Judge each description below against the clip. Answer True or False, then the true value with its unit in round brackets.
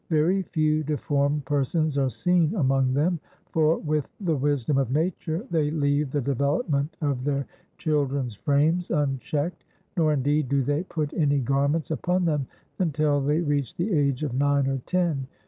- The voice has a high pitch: False (145 Hz)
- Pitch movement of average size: False (2.2 semitones)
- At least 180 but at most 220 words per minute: False (160 wpm)